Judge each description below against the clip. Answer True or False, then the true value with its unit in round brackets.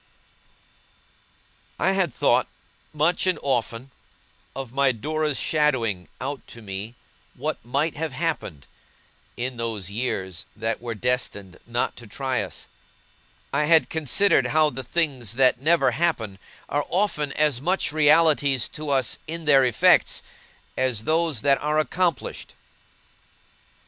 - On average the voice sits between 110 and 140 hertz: True (135 Hz)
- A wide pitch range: False (4.7 semitones)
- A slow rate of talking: True (130 wpm)